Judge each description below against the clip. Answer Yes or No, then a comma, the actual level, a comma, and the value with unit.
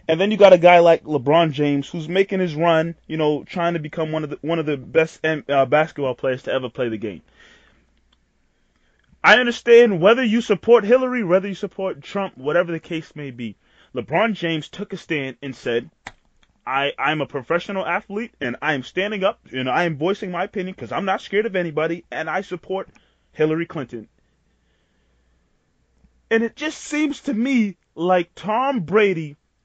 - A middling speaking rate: Yes, average, 180 wpm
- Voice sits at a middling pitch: Yes, medium, 165 Hz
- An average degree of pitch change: No, wide, 5.8 semitones